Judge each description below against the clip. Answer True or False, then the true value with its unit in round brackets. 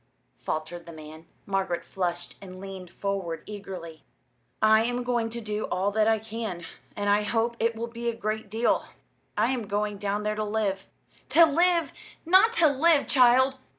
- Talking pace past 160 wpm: True (175 wpm)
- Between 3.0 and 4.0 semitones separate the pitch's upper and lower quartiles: True (3.5 semitones)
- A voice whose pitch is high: True (215 Hz)